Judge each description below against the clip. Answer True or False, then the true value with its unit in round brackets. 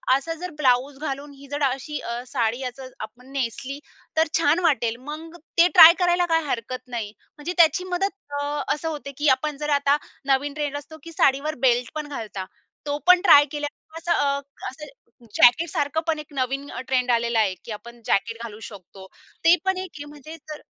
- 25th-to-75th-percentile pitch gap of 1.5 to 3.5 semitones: False (4.0 semitones)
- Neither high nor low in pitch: False (285 Hz)